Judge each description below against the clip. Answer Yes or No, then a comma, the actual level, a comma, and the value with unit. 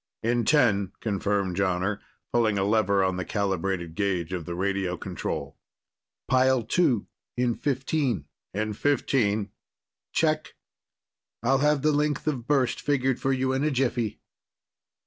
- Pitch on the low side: Yes, low, 110 Hz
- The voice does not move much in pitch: No, wide, 5.4 semitones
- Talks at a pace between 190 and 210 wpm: No, slow, 135 wpm